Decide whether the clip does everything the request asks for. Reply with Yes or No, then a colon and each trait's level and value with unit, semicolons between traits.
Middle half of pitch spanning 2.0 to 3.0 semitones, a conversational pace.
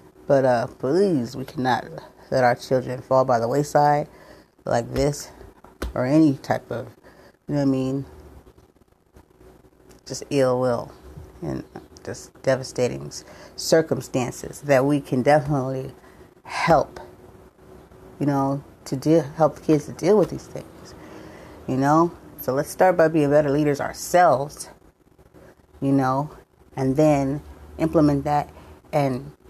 No: narrow, 2.6 semitones; slow, 130 wpm